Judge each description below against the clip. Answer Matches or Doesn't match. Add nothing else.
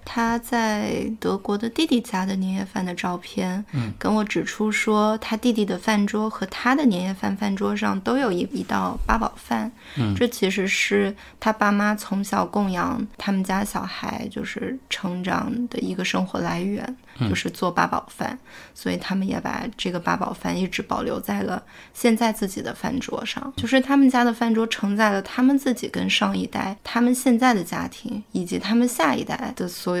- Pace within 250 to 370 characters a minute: Matches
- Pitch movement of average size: Matches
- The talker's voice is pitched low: Doesn't match